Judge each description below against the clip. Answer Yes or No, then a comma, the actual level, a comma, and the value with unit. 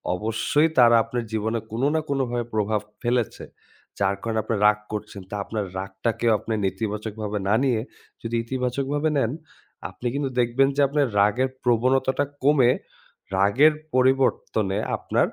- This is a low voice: Yes, low, 120 Hz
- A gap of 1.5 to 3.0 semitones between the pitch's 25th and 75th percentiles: No, average, 3.7 semitones